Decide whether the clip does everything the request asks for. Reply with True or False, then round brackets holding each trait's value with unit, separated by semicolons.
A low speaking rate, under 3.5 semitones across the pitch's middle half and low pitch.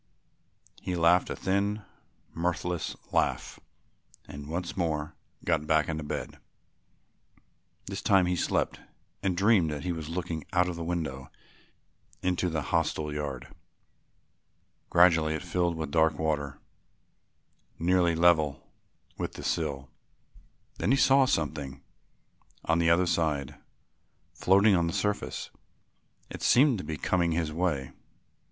True (130 wpm; 2.8 semitones; 85 Hz)